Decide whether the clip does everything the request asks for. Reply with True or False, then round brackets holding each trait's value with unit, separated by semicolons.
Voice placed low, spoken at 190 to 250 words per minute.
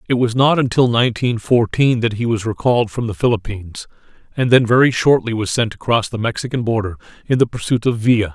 True (115 Hz; 200 wpm)